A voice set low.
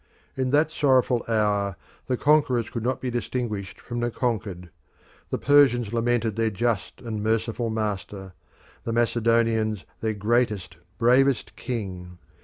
Yes: low, 115 Hz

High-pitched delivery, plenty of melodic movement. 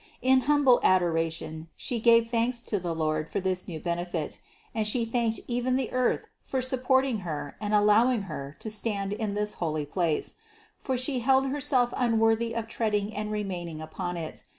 Yes: high, 215 Hz; wide, 5.8 semitones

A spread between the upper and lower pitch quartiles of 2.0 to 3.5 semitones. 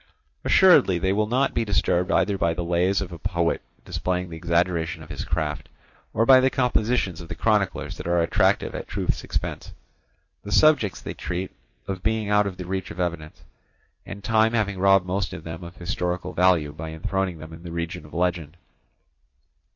Yes: average, 3.1 semitones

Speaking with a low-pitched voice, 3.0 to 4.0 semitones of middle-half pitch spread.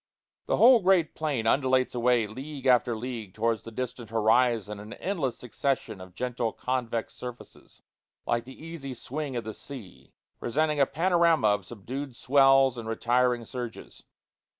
Yes: low, 125 Hz; average, 3.3 semitones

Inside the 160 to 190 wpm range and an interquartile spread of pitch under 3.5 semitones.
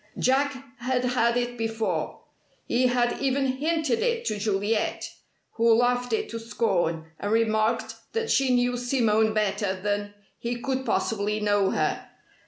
No: average, 145 wpm; average, 3.1 semitones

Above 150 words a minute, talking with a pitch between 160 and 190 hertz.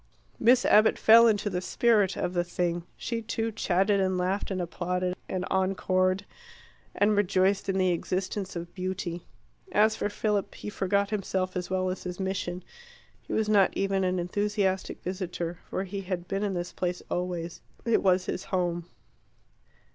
Yes: average, 165 wpm; medium, 185 Hz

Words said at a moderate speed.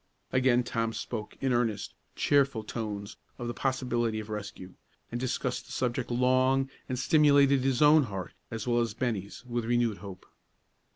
Yes: average, 160 wpm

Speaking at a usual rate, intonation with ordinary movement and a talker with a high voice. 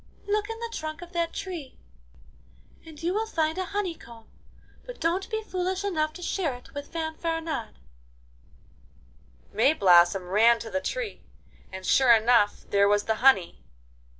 No: average, 150 wpm; wide, 8.2 semitones; very high, 315 Hz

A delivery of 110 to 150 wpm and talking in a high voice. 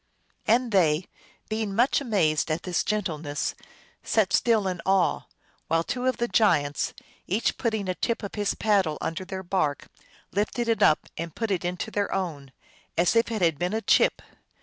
No: average, 185 wpm; high, 195 Hz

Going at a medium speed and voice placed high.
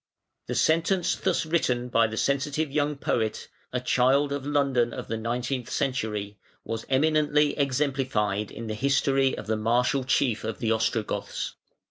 No: average, 150 wpm; low, 130 Hz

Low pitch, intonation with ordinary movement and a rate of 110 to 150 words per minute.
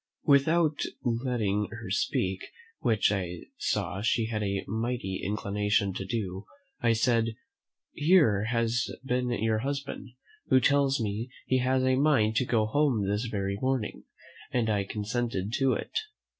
Yes: low, 115 Hz; average, 4.0 semitones; average, 145 wpm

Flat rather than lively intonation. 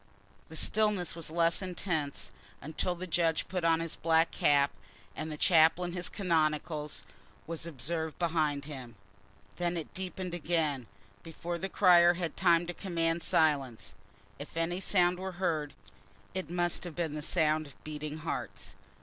Yes: narrow, 2.3 semitones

